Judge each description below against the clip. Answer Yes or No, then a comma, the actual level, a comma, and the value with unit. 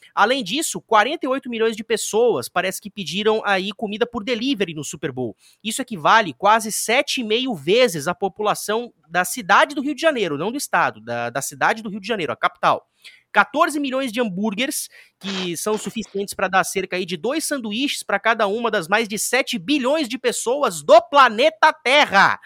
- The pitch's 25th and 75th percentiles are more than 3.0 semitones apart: Yes, average, 5.2 semitones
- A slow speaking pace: No, fast, 185 wpm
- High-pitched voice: Yes, high, 220 Hz